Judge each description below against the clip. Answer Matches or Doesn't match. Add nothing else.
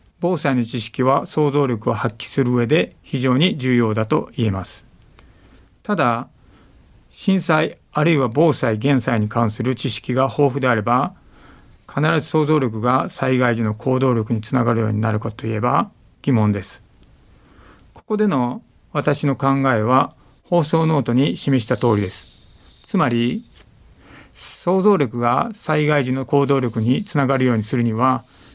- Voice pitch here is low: Matches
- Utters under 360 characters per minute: Matches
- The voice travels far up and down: Doesn't match